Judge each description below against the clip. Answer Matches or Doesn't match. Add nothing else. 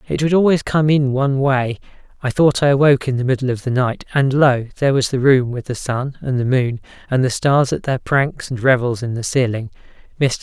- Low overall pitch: Matches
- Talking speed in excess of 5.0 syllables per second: Matches